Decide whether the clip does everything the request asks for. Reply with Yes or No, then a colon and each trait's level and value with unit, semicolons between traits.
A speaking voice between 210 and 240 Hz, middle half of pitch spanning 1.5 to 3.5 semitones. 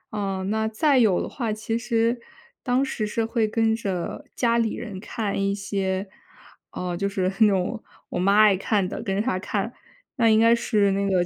Yes: high, 215 Hz; average, 2.8 semitones